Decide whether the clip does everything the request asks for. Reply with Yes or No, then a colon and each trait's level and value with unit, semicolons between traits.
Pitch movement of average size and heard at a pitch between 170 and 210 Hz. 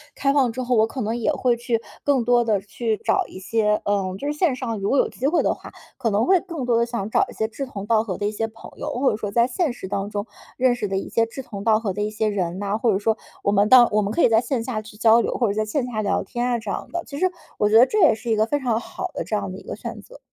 No: average, 3.1 semitones; high, 225 Hz